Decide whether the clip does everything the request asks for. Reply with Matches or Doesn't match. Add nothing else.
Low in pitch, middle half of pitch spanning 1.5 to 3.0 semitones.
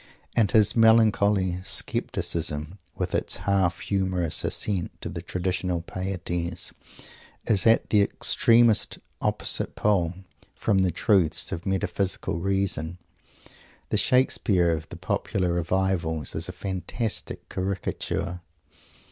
Matches